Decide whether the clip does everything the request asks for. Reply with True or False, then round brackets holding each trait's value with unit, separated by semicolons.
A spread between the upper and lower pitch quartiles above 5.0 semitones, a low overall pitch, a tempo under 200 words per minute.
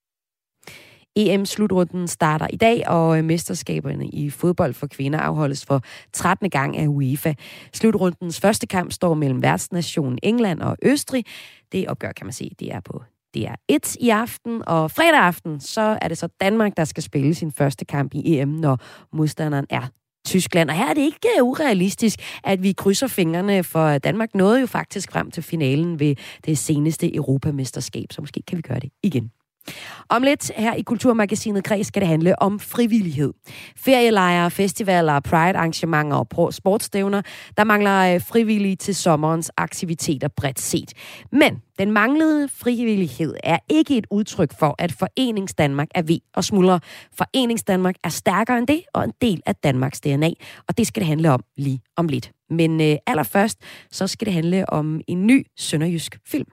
False (5.4 semitones; 175 Hz; 170 wpm)